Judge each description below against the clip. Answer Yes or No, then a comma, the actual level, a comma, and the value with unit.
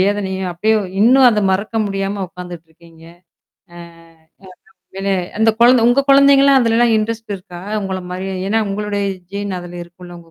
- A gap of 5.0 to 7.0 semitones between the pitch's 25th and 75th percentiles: No, average, 3.8 semitones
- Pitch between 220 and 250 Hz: No, high, 200 Hz